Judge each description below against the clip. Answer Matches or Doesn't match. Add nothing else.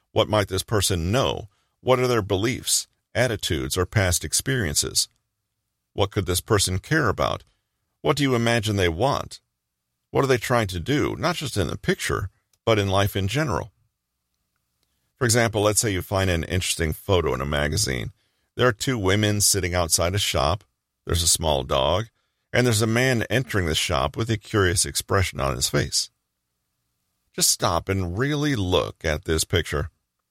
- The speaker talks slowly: Doesn't match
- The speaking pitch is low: Matches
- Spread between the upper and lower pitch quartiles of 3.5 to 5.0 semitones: Doesn't match